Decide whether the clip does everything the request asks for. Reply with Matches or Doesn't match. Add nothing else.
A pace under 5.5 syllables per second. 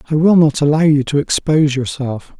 Doesn't match